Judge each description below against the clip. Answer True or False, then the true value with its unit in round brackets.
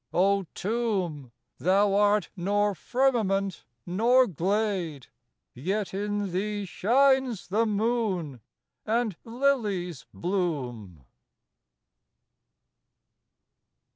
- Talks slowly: True (75 wpm)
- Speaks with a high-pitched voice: True (200 Hz)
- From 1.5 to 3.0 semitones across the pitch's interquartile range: False (3.8 semitones)